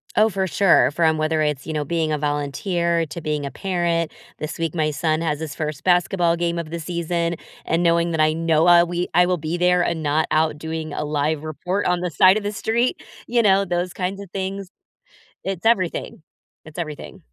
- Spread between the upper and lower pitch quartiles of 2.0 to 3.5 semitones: Yes, narrow, 2.4 semitones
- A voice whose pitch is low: No, medium, 170 Hz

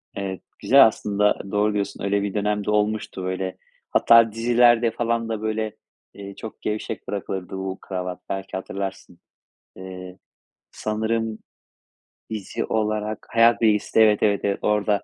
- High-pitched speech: No, low, 105 Hz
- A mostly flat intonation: Yes, narrow, 2.2 semitones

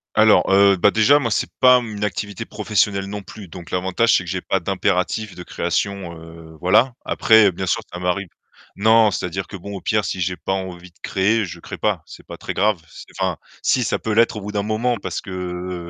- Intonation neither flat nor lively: Yes, average, 3.1 semitones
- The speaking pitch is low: Yes, very low, 95 Hz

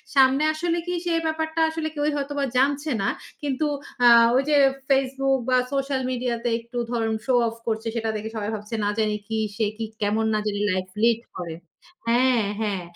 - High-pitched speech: Yes, high, 245 Hz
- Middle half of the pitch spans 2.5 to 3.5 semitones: No, average, 4.1 semitones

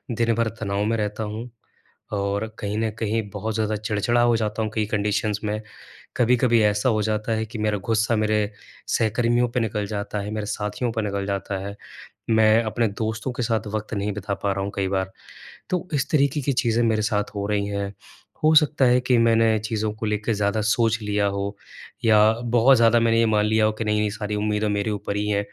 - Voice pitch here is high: No, low, 110 Hz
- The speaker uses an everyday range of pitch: No, narrow, 1.7 semitones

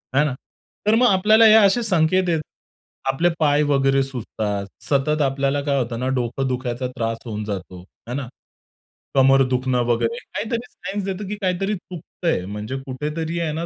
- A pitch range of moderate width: No, wide, 6.5 semitones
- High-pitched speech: No, medium, 140 Hz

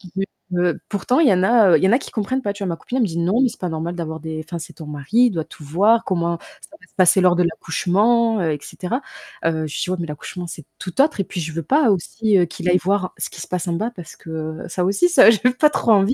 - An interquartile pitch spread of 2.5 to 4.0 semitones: No, average, 4.7 semitones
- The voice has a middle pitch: Yes, medium, 180 Hz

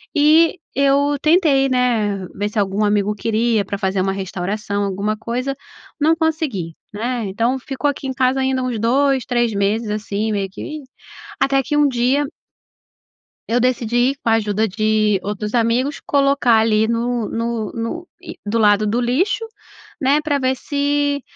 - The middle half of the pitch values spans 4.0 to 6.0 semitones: Yes, average, 4.6 semitones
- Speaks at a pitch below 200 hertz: No, high, 235 Hz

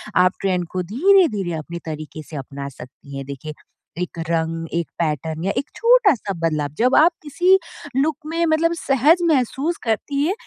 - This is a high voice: Yes, high, 195 Hz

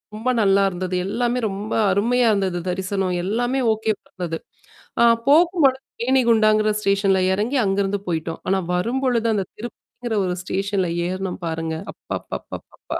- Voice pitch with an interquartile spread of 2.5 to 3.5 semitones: No, average, 4.0 semitones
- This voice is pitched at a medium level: No, high, 205 Hz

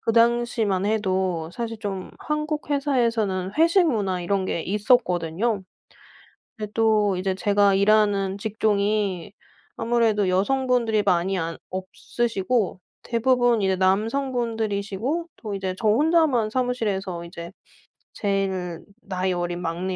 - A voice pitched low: No, high, 205 Hz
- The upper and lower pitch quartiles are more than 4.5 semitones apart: No, average, 3.8 semitones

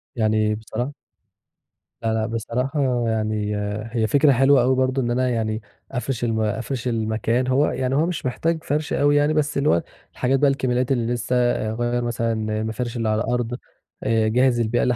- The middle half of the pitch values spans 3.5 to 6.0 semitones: No, average, 3.0 semitones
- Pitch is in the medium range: No, low, 120 Hz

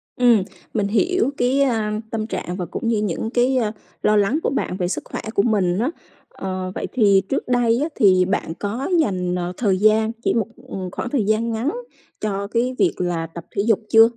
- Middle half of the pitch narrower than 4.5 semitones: Yes, average, 3.9 semitones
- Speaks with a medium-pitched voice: No, high, 215 Hz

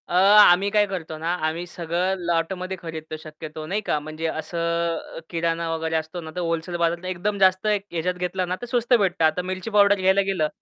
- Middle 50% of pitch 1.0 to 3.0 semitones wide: Yes, average, 2.7 semitones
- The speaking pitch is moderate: Yes, medium, 175 Hz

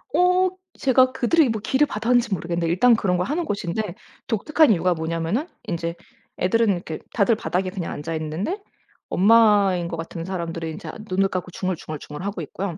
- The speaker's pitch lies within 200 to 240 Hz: No, high, 190 Hz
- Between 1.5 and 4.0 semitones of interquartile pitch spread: No, wide, 5.4 semitones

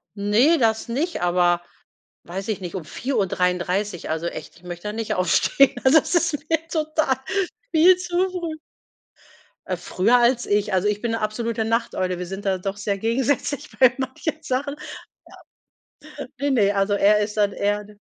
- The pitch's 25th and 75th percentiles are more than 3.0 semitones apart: Yes, wide, 5.6 semitones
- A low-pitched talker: No, high, 215 Hz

